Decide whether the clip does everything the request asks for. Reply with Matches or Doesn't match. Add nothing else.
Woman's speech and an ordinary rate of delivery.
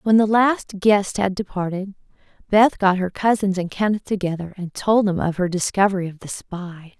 Matches